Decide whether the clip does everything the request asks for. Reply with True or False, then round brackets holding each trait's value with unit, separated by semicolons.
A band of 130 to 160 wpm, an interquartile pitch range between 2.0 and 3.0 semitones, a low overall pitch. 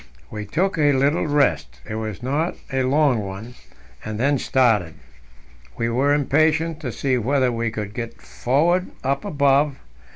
False (155 wpm; 4.5 semitones; 130 Hz)